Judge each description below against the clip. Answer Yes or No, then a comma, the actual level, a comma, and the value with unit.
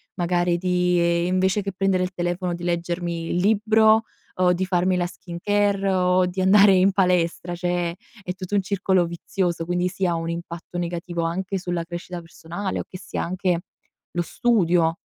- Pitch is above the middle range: No, medium, 180 Hz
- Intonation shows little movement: Yes, narrow, 1.6 semitones